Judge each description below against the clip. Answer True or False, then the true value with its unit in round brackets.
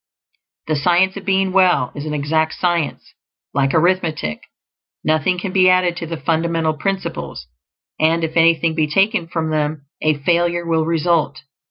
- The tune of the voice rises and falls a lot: False (2.4 semitones)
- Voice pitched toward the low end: False (165 Hz)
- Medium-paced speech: True (155 wpm)